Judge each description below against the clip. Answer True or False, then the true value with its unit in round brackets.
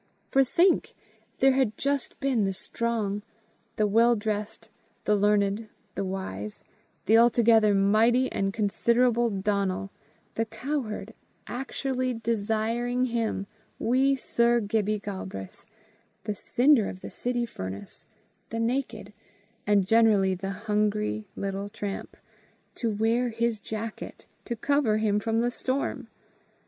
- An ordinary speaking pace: False (120 wpm)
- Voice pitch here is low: False (220 Hz)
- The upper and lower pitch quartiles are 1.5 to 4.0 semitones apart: True (2.8 semitones)